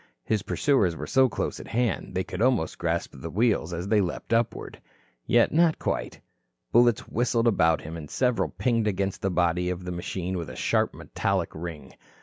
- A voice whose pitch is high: No, low, 100 Hz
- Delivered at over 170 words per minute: Yes, average, 185 wpm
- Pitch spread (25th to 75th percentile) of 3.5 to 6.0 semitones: Yes, average, 5.3 semitones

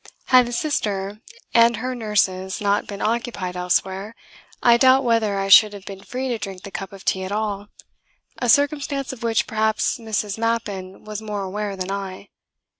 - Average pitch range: Yes, average, 3.2 semitones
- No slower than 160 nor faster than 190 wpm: Yes, average, 180 wpm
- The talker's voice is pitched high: Yes, high, 210 Hz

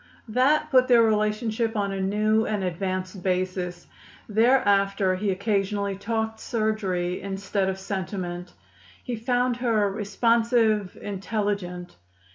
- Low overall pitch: No, high, 205 Hz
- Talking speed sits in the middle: No, slow, 110 wpm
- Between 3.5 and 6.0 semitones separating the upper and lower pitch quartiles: No, average, 2.7 semitones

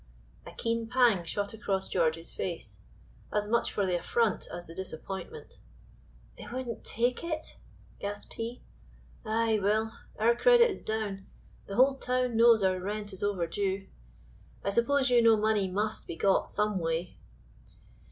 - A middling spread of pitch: Yes, average, 3.6 semitones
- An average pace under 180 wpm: Yes, average, 150 wpm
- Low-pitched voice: No, high, 210 Hz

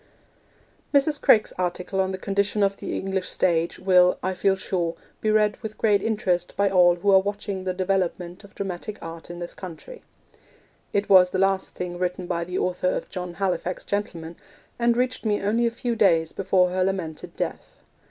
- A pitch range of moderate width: No, narrow, 2.2 semitones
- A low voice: No, high, 190 Hz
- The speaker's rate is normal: Yes, average, 185 wpm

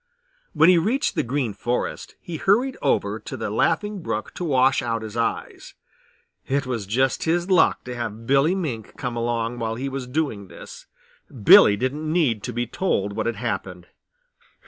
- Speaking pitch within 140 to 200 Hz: No, low, 125 Hz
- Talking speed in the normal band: Yes, average, 175 wpm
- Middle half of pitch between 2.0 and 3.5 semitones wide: No, wide, 5.6 semitones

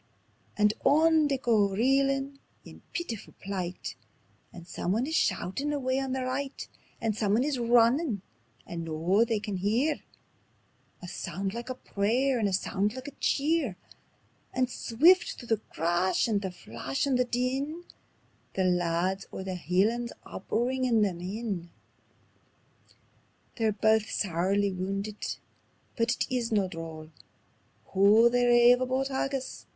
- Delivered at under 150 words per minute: Yes, average, 140 wpm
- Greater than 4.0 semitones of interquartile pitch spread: Yes, average, 5.2 semitones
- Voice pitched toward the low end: No, high, 225 Hz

